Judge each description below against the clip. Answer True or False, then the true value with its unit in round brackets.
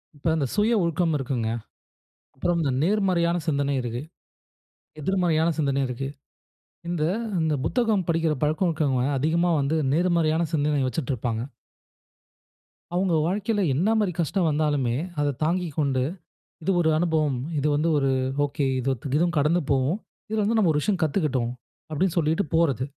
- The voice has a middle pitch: True (155 Hz)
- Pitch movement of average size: True (4.0 semitones)